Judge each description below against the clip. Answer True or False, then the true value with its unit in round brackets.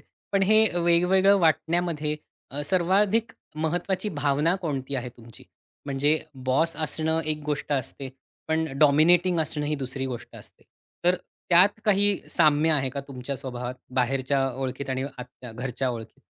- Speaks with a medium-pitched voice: True (150 Hz)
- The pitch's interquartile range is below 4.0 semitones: False (4.7 semitones)